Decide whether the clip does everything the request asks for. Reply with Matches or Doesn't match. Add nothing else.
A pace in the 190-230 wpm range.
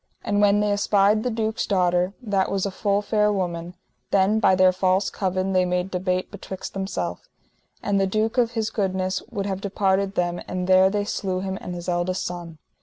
Matches